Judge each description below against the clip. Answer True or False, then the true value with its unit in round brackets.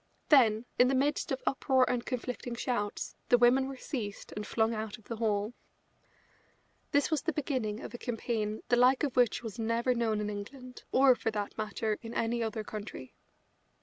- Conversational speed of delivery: True (185 wpm)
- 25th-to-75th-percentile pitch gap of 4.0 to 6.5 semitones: False (3.0 semitones)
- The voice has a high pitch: True (235 Hz)